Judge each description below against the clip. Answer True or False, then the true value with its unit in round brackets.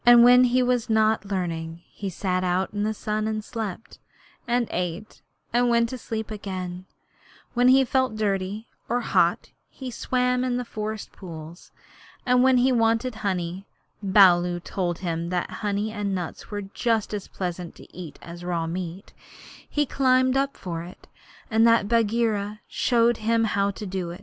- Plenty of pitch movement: False (4.4 semitones)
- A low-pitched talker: False (210 Hz)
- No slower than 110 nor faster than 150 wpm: False (165 wpm)